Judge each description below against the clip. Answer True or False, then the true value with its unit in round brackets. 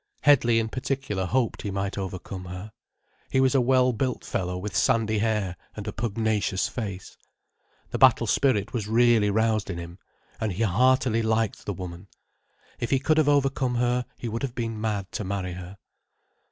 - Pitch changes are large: False (3.9 semitones)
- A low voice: True (110 Hz)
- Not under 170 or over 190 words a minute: True (180 wpm)